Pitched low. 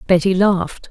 No: medium, 185 Hz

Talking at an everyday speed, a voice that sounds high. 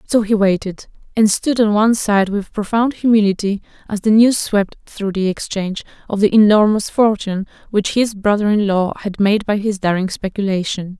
Yes: average, 180 wpm; high, 205 Hz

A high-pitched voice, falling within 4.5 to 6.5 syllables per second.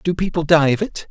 No: medium, 165 Hz; 5.6 syllables/s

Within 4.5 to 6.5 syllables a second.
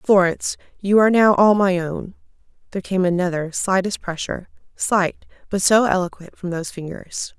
Yes: 5.3 syllables/s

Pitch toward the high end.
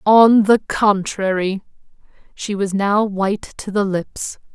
Yes: high, 200 Hz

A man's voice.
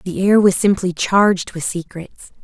No: female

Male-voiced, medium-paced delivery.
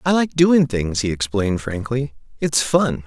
Yes: male; average, 175 wpm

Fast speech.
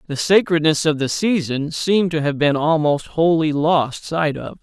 No: average, 180 wpm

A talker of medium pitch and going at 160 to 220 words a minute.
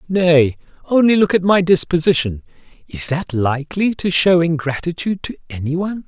No: medium, 165 Hz; average, 140 wpm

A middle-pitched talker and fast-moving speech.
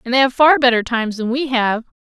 No: very high, 250 Hz; fast, 265 wpm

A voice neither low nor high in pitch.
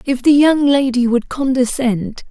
No: very high, 255 Hz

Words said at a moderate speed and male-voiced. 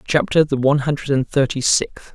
Yes: average, 195 wpm; male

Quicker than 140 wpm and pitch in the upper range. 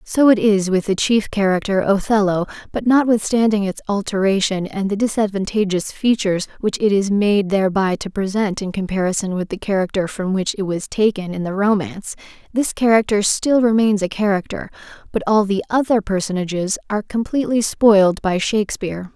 Yes: average, 165 wpm; high, 205 Hz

